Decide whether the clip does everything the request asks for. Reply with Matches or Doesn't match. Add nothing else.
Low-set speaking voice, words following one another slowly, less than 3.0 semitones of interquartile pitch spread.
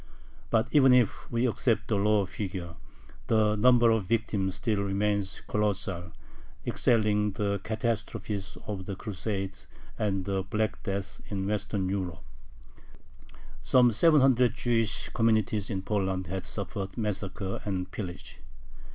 Matches